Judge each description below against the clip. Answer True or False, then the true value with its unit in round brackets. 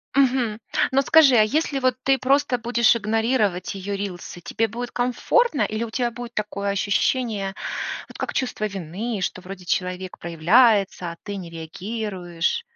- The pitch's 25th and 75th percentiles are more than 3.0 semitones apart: True (4.6 semitones)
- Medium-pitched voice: False (215 Hz)